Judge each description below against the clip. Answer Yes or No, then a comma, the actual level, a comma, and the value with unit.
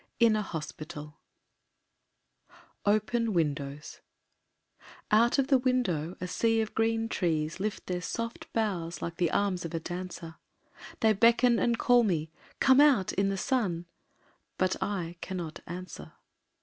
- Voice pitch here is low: No, high, 190 Hz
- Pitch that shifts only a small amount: No, wide, 5.4 semitones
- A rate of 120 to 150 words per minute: Yes, average, 140 wpm